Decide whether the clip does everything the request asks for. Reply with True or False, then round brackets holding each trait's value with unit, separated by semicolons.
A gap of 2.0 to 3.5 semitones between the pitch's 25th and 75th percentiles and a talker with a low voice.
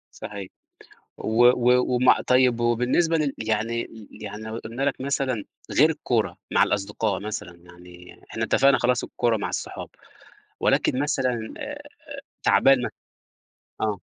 True (3.2 semitones; 115 Hz)